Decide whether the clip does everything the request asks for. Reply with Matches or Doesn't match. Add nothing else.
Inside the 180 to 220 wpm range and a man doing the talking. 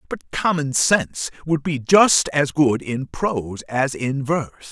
Doesn't match